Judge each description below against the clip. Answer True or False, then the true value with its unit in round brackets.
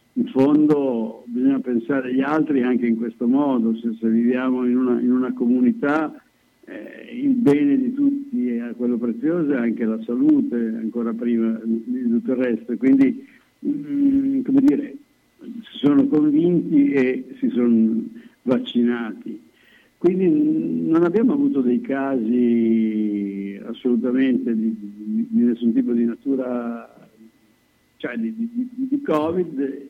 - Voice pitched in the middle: False (130 Hz)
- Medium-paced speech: True (130 wpm)